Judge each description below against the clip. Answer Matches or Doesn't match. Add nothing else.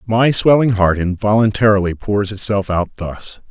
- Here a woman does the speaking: Doesn't match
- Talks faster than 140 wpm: Doesn't match